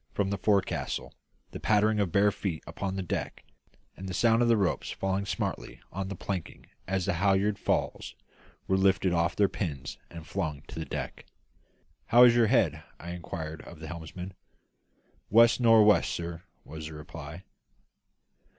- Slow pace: No, average, 165 wpm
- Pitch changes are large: No, average, 3.6 semitones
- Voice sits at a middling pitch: No, very low, 95 Hz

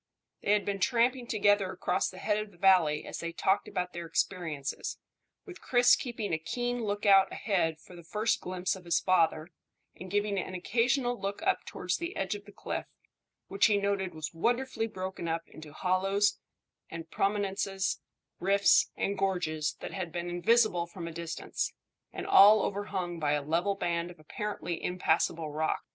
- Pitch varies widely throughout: No, average, 3.3 semitones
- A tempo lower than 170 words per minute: No, average, 175 wpm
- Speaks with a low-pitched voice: No, high, 190 Hz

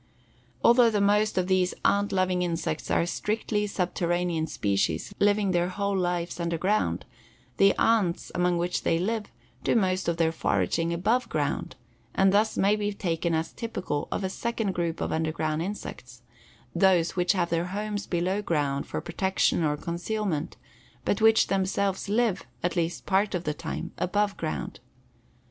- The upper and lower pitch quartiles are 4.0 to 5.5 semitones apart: No, average, 3.3 semitones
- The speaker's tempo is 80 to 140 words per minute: No, average, 160 wpm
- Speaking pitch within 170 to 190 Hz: Yes, medium, 185 Hz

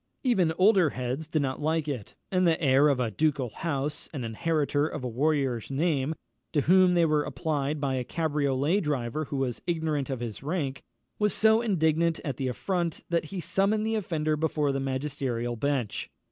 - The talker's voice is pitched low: No, medium, 150 Hz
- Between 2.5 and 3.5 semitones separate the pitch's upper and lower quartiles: No, average, 3.9 semitones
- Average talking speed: Yes, average, 185 wpm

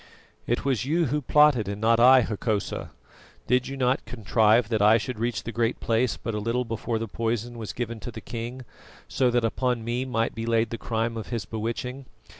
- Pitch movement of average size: No, narrow, 1.9 semitones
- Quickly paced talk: Yes, fast, 210 wpm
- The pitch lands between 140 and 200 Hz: No, low, 115 Hz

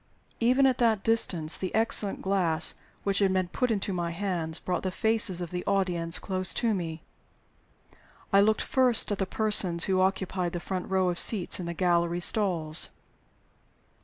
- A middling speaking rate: Yes, average, 170 wpm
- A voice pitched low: No, medium, 185 Hz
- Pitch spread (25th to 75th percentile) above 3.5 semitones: No, average, 3.1 semitones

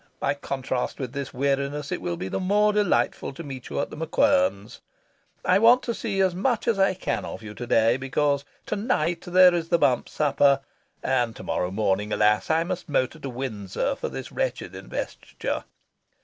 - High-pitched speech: No, medium, 145 Hz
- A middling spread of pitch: No, wide, 6.9 semitones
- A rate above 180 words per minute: Yes, average, 190 wpm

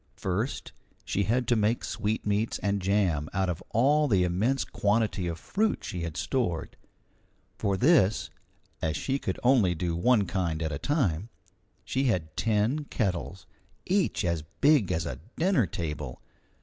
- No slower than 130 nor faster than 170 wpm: Yes, average, 150 wpm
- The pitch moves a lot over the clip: Yes, wide, 6.1 semitones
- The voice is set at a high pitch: No, low, 100 Hz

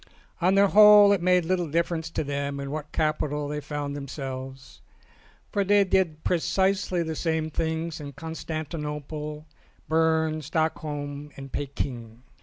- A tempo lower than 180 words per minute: Yes, average, 140 wpm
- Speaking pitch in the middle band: Yes, medium, 155 Hz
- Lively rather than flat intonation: No, average, 2.8 semitones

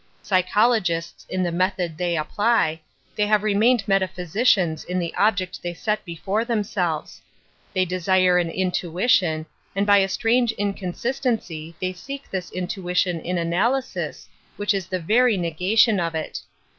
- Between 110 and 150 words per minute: Yes, average, 145 wpm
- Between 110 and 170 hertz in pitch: No, medium, 185 Hz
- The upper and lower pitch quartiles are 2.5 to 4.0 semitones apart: Yes, average, 3.4 semitones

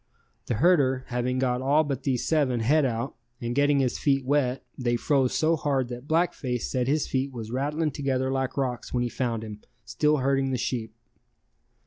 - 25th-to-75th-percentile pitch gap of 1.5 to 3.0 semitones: Yes, narrow, 2.6 semitones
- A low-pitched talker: Yes, low, 130 Hz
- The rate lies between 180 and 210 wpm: Yes, average, 190 wpm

